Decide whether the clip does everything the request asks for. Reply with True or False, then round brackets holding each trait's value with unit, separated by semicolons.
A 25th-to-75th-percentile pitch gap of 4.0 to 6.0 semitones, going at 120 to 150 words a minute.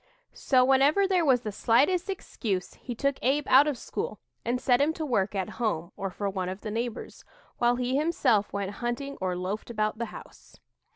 False (5.3 semitones; 195 wpm)